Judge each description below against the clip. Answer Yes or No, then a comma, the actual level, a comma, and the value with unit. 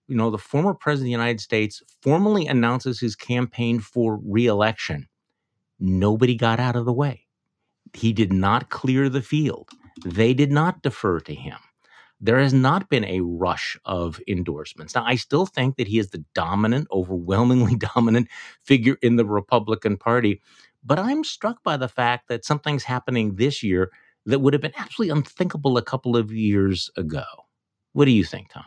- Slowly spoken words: No, average, 175 wpm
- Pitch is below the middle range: Yes, low, 120 Hz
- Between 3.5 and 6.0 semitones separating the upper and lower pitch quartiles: Yes, average, 4.1 semitones